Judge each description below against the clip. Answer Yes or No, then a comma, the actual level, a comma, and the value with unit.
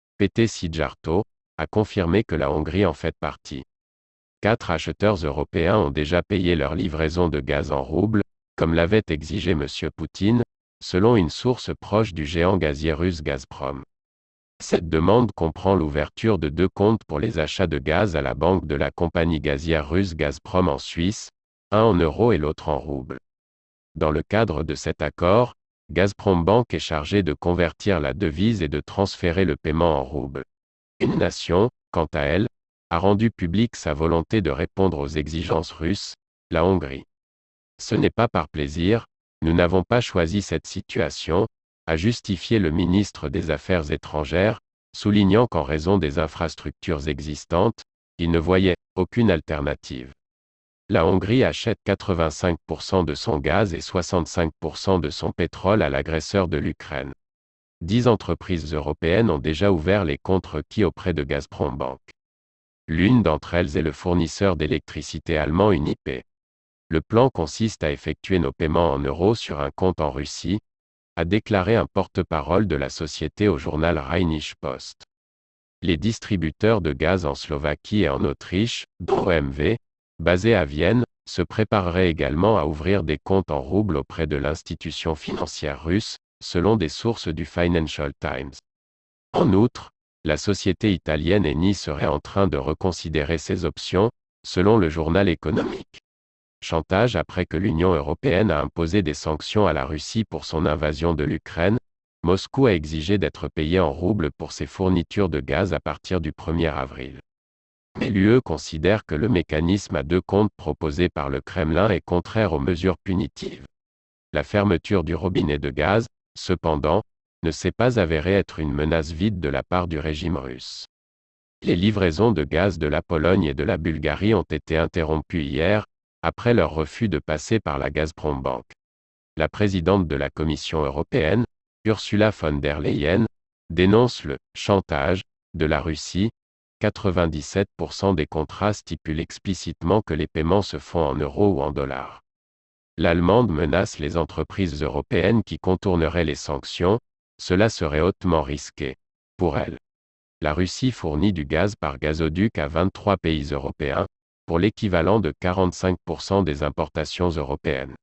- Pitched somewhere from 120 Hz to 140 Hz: No, very low, 85 Hz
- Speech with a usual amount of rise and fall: Yes, average, 4.5 semitones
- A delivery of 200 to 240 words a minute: No, average, 155 wpm